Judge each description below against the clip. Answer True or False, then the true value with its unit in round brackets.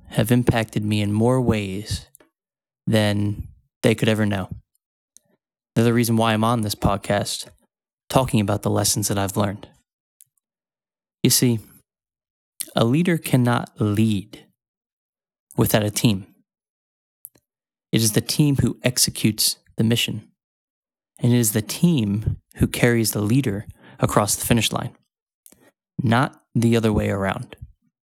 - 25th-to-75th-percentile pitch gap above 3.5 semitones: False (2.7 semitones)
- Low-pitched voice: True (110 Hz)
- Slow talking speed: True (130 wpm)